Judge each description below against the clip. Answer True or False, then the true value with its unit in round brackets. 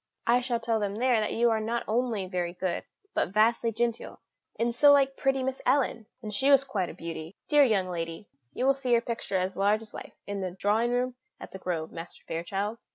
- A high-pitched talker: True (225 Hz)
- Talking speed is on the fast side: True (225 wpm)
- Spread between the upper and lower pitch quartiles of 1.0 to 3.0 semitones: False (4.3 semitones)